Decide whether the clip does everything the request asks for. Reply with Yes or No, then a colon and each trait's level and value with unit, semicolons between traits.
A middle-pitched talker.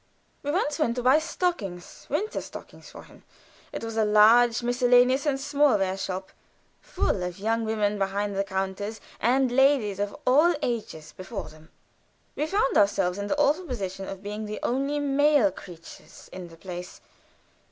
No: high, 220 Hz